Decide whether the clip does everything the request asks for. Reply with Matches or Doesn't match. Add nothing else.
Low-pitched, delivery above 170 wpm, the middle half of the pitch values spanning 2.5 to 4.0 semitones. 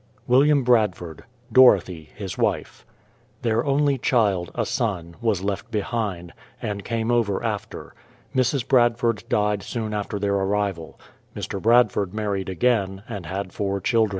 Doesn't match